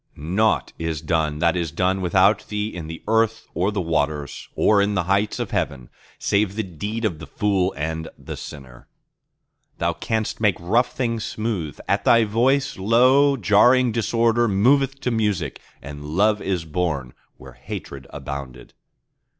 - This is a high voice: No, low, 100 Hz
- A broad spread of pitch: Yes, wide, 5.7 semitones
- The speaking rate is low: No, average, 160 wpm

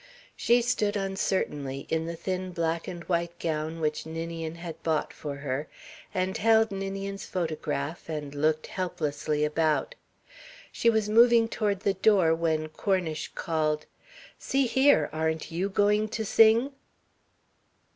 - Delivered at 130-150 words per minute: Yes, slow, 135 wpm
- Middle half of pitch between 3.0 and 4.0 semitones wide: No, average, 4.5 semitones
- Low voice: No, medium, 170 Hz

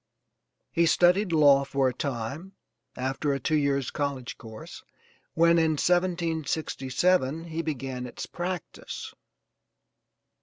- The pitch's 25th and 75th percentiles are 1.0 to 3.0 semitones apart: No, average, 3.9 semitones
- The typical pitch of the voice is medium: Yes, medium, 150 Hz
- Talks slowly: Yes, slow, 110 wpm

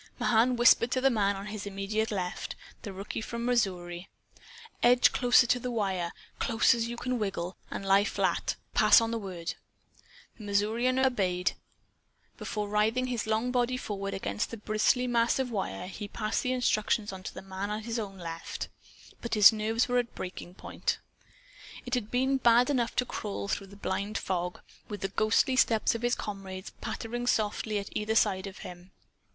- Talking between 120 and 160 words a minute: No, average, 180 wpm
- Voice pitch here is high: Yes, high, 215 Hz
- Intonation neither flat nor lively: Yes, average, 3.5 semitones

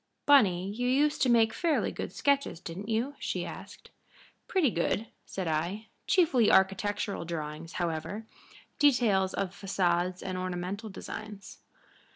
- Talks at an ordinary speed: No, slow, 130 wpm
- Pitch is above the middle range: Yes, high, 200 Hz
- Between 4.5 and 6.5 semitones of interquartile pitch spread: Yes, average, 5.0 semitones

